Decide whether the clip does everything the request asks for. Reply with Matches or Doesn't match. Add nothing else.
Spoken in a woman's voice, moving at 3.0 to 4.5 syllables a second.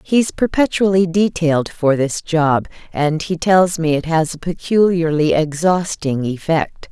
Matches